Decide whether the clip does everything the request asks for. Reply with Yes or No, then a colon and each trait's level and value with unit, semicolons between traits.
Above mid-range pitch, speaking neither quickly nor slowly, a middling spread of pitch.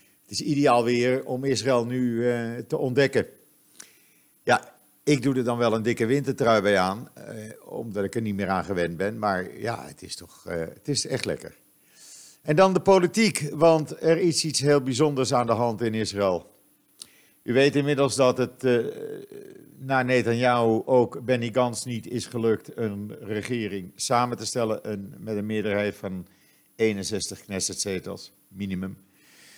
No: low, 120 Hz; average, 165 wpm; average, 4.6 semitones